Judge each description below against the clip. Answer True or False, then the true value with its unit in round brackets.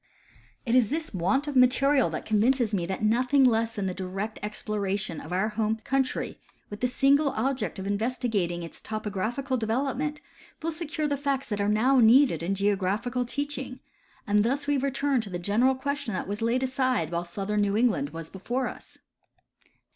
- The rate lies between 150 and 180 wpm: True (175 wpm)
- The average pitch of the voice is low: False (230 Hz)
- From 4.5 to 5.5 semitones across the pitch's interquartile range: True (4.8 semitones)